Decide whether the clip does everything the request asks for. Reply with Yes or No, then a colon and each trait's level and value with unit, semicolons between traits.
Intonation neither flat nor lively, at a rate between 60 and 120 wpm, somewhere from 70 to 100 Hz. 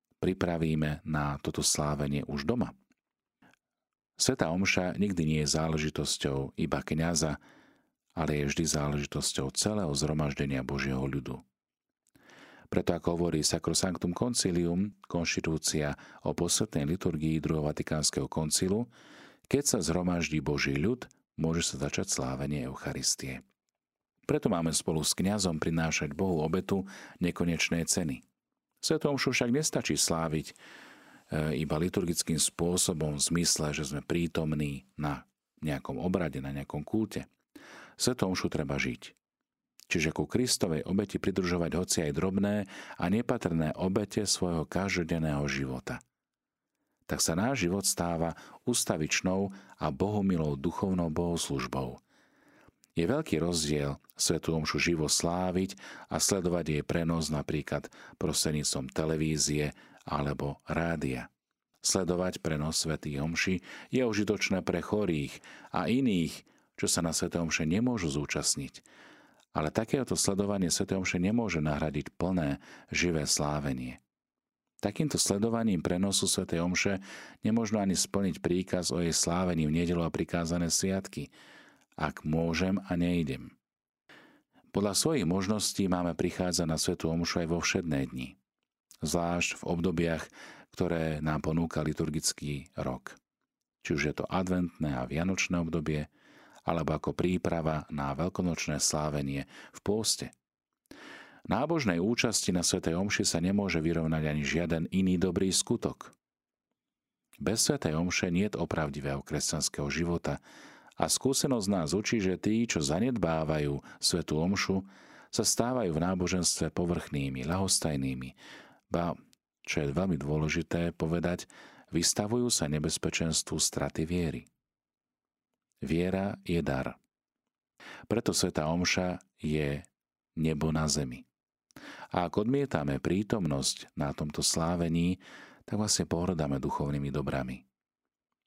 Yes: average, 3.5 semitones; average, 115 wpm; very low, 80 Hz